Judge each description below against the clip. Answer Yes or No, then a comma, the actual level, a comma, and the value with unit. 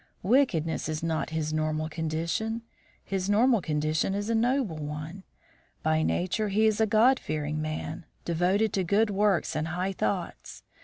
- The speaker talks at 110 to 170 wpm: Yes, average, 155 wpm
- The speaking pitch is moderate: Yes, medium, 175 Hz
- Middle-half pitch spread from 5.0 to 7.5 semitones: Yes, wide, 5.4 semitones